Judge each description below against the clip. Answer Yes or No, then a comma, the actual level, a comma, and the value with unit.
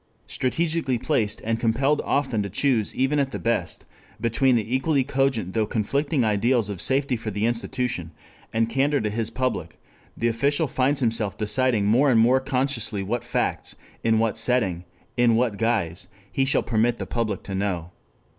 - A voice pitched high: No, low, 115 Hz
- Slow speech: No, average, 170 wpm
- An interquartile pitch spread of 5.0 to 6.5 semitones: No, average, 3.5 semitones